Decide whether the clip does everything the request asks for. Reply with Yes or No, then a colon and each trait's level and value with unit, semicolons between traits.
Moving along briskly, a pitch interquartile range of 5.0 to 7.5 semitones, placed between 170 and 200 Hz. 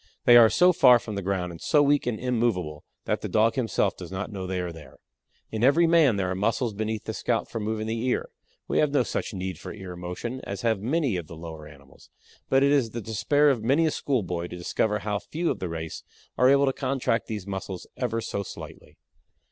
No: fast, 235 wpm; wide, 5.4 semitones; low, 110 Hz